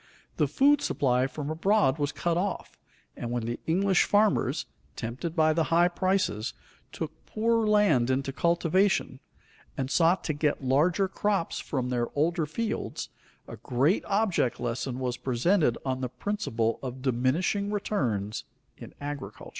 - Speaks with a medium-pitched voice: Yes, medium, 155 Hz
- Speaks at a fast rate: No, average, 145 wpm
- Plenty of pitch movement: Yes, wide, 6.8 semitones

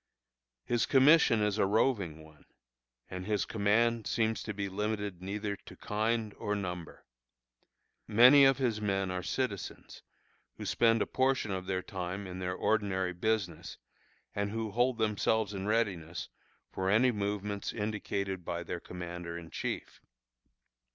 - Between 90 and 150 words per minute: Yes, average, 145 wpm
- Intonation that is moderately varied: Yes, average, 3.2 semitones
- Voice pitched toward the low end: Yes, low, 105 Hz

